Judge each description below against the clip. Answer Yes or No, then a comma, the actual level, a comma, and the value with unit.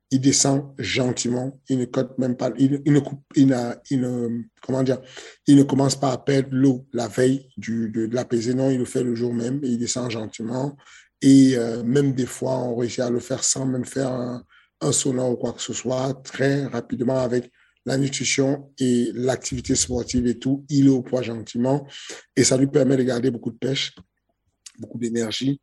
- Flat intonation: Yes, narrow, 1.8 semitones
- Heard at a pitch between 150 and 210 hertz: No, low, 130 Hz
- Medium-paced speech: Yes, average, 185 wpm